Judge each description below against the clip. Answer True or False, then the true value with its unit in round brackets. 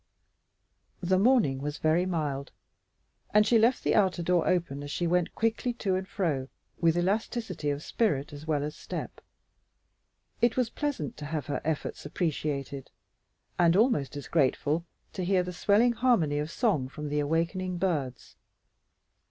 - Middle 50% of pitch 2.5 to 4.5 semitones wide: False (5.3 semitones)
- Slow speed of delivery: False (155 wpm)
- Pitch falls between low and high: True (170 Hz)